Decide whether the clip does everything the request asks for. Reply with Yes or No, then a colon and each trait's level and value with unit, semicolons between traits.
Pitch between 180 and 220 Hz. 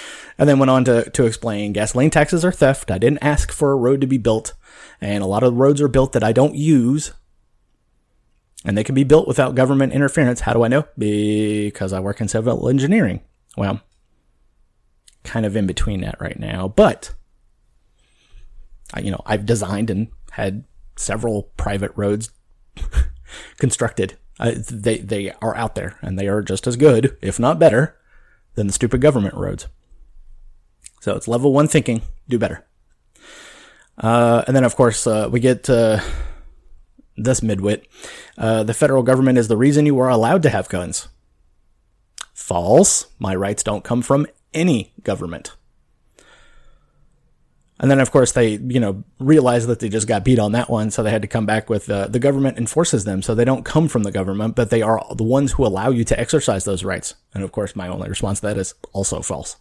No: low, 115 Hz